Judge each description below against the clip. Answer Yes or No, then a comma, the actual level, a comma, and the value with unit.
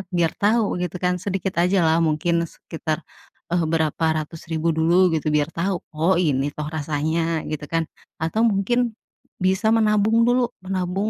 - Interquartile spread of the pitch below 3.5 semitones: No, average, 3.8 semitones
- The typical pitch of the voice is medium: Yes, medium, 175 Hz